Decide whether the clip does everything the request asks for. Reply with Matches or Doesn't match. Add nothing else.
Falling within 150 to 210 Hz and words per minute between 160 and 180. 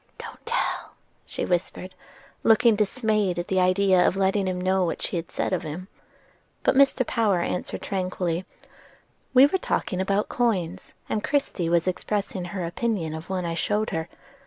Matches